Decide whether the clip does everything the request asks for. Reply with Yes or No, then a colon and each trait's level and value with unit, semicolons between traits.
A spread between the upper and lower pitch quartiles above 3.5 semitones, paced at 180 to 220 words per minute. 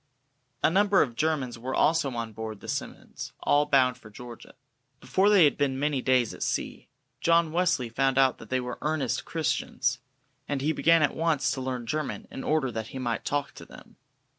Yes: average, 4.1 semitones; average, 195 wpm